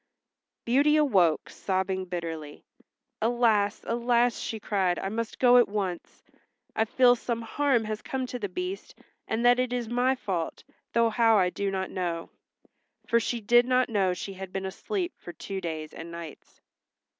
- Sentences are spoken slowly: No, average, 170 wpm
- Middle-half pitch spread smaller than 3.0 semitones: No, average, 4.6 semitones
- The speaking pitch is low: No, high, 220 Hz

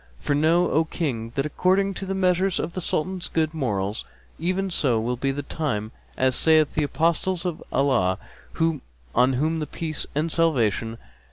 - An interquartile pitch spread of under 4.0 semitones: No, average, 4.8 semitones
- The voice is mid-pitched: Yes, medium, 155 Hz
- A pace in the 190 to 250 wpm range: No, average, 170 wpm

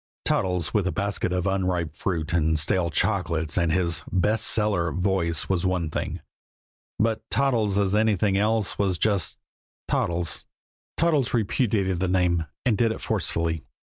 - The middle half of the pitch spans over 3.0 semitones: Yes, average, 3.6 semitones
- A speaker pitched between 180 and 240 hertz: No, very low, 95 Hz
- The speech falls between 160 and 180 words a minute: No, average, 150 wpm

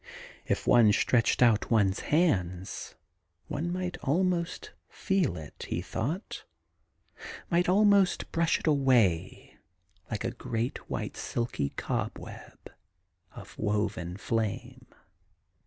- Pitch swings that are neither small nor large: No, wide, 8.5 semitones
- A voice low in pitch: Yes, low, 120 Hz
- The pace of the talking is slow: Yes, slow, 105 wpm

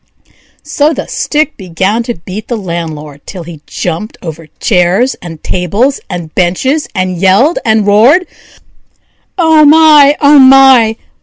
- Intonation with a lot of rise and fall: Yes, wide, 7.9 semitones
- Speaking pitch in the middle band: No, high, 210 Hz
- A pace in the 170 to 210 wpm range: No, slow, 135 wpm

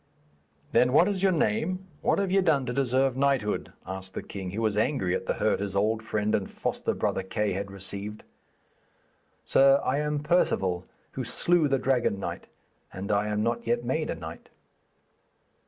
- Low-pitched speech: Yes, low, 115 Hz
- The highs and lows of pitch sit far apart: Yes, wide, 5.7 semitones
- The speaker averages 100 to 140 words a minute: No, average, 180 wpm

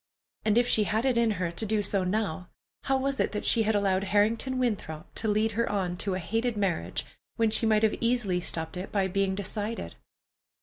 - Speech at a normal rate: No, fast, 215 wpm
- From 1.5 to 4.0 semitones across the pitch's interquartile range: Yes, average, 3.0 semitones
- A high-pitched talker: Yes, high, 210 Hz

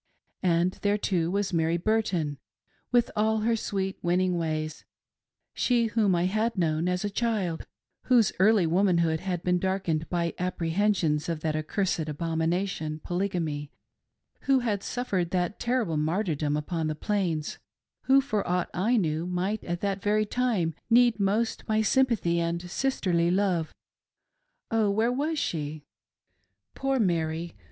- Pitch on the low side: No, medium, 180 Hz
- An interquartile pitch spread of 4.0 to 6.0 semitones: Yes, average, 4.4 semitones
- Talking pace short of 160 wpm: Yes, average, 150 wpm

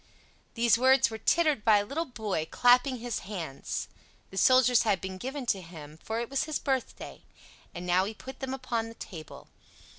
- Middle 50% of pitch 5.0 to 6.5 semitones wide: Yes, wide, 5.4 semitones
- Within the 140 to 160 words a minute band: No, average, 185 wpm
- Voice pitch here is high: Yes, high, 230 Hz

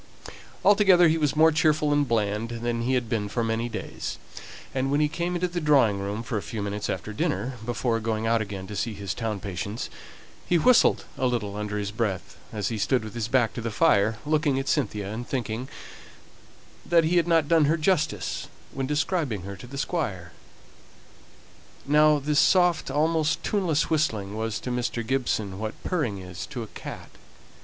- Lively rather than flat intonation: Yes, wide, 6.1 semitones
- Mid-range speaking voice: No, low, 120 Hz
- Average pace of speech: Yes, average, 190 wpm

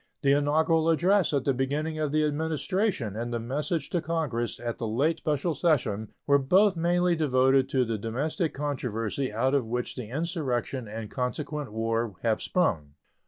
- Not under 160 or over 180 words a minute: Yes, average, 165 wpm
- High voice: No, medium, 140 Hz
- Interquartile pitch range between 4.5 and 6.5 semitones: Yes, average, 5.2 semitones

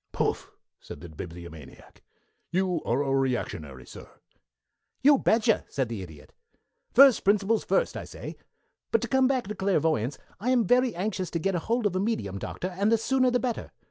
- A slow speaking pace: No, average, 175 wpm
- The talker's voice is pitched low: No, high, 190 Hz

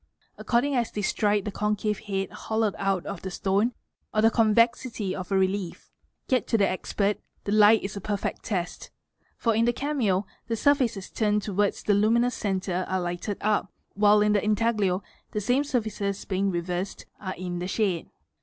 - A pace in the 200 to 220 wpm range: No, average, 175 wpm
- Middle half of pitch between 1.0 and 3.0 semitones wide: Yes, narrow, 2.6 semitones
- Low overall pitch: No, high, 205 Hz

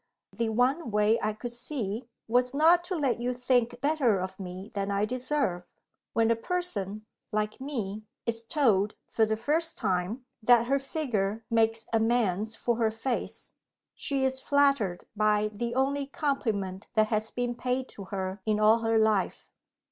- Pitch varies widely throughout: No, average, 3.6 semitones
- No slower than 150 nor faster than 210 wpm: Yes, average, 165 wpm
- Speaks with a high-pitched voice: Yes, high, 230 Hz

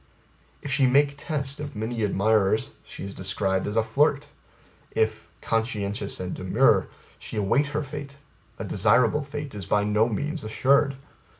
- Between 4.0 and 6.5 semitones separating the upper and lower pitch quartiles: Yes, average, 5.3 semitones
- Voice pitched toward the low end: Yes, low, 115 Hz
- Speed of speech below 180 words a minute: Yes, average, 155 wpm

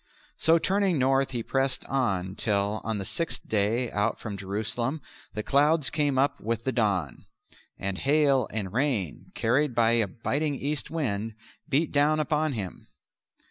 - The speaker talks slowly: No, average, 155 wpm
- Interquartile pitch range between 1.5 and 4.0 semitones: No, wide, 5.4 semitones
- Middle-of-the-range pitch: No, low, 125 Hz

